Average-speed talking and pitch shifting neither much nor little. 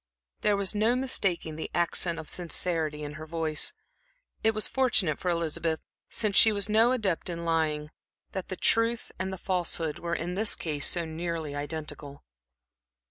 Yes: average, 165 wpm; average, 4.2 semitones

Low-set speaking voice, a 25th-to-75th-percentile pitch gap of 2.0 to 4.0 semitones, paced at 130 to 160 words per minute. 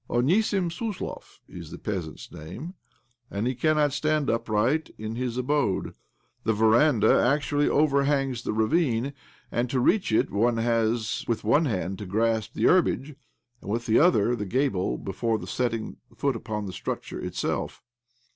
No: low, 120 Hz; average, 4.8 semitones; average, 150 wpm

